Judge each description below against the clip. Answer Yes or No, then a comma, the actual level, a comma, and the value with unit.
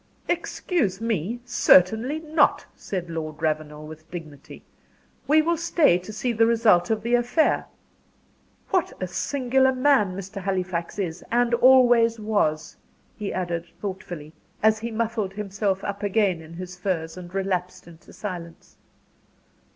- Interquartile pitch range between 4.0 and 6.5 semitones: Yes, average, 5.1 semitones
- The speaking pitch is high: Yes, high, 195 Hz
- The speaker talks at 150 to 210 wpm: No, slow, 135 wpm